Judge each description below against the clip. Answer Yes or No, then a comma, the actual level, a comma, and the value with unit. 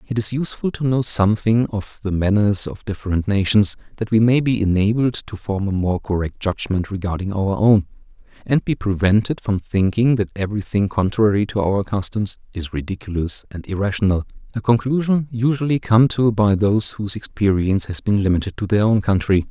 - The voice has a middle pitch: No, low, 105 Hz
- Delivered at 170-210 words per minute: Yes, average, 175 wpm